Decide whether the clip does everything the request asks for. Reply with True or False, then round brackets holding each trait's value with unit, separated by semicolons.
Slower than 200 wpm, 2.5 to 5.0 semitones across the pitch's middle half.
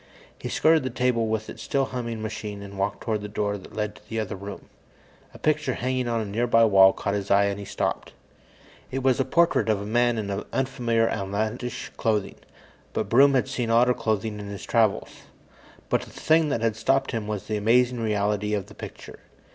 False (205 wpm; 3.3 semitones)